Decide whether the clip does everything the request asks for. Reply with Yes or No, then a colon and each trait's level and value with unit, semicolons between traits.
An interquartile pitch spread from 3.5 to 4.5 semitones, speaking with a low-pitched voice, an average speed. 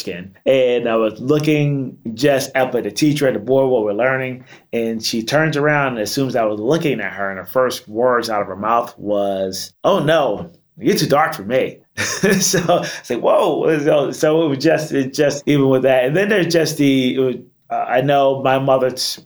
No: average, 4.1 semitones; low, 130 Hz; fast, 220 wpm